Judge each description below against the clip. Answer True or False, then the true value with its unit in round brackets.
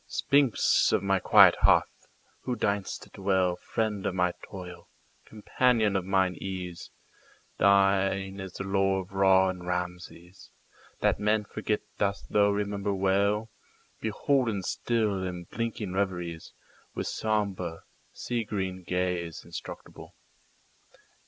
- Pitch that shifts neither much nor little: False (2.2 semitones)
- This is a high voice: False (95 Hz)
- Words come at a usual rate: False (105 wpm)